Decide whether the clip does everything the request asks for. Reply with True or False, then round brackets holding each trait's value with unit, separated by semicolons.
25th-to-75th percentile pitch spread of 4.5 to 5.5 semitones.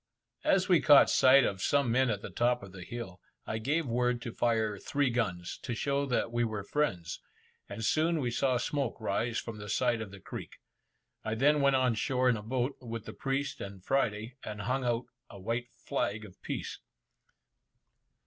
False (3.9 semitones)